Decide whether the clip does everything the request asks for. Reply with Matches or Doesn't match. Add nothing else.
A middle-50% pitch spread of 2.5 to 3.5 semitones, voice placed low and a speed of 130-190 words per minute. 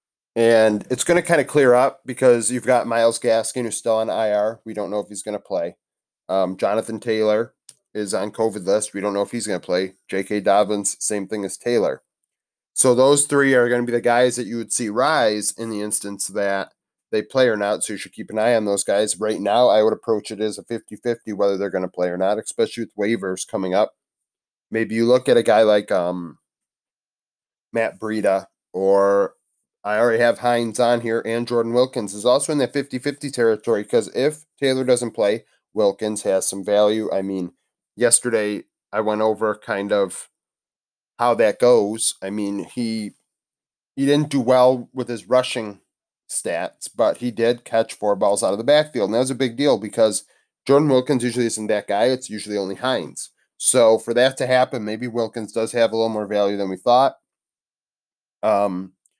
Doesn't match